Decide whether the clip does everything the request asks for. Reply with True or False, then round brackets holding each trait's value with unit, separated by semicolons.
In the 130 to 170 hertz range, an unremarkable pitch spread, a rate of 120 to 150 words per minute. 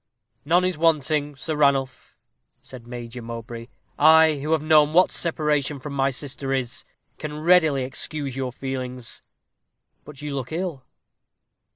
True (140 Hz; 3.1 semitones; 140 wpm)